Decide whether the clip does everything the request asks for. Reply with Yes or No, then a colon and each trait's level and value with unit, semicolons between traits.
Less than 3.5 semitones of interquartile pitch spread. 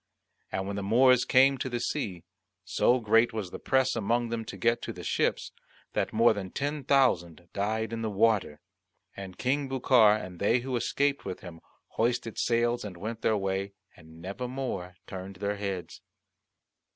No: average, 4.2 semitones